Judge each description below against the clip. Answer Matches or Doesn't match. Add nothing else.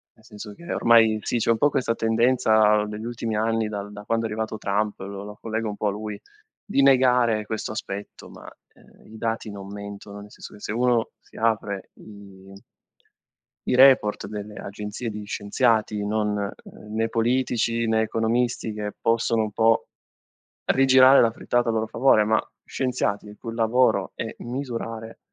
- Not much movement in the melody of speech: Matches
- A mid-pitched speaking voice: Doesn't match